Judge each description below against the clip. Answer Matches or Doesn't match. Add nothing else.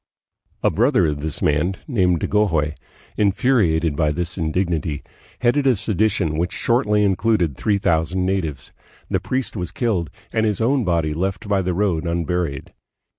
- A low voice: Matches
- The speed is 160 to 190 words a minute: Doesn't match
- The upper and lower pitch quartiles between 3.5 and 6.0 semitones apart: Matches